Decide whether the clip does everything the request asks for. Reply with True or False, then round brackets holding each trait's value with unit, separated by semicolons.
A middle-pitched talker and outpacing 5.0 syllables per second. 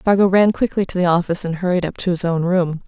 True (180 Hz; 6.4 syllables/s)